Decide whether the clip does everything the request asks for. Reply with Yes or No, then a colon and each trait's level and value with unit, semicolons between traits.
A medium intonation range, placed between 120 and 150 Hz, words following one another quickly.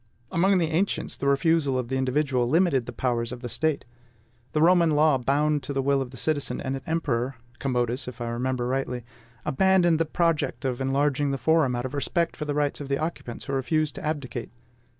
Yes: average, 3.6 semitones; medium, 140 Hz; fast, 210 wpm